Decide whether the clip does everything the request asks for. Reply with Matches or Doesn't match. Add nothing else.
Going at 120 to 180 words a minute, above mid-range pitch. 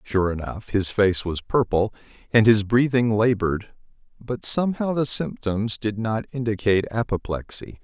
Doesn't match